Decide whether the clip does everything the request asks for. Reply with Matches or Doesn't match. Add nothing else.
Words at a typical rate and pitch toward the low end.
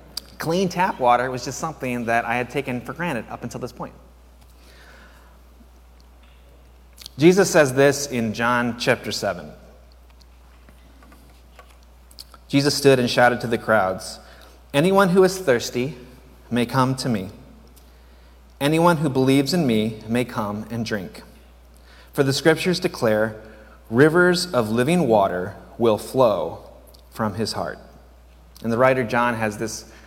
Doesn't match